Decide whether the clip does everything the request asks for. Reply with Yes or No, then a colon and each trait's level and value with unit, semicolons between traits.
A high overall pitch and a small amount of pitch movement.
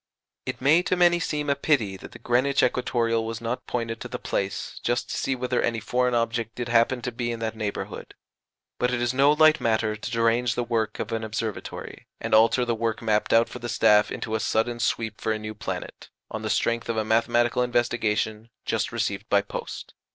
No: low, 115 Hz; narrow, 1.8 semitones